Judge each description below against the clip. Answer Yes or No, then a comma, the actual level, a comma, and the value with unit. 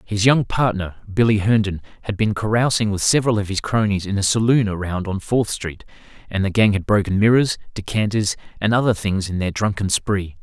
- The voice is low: Yes, low, 105 Hz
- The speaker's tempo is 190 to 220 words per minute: Yes, average, 195 wpm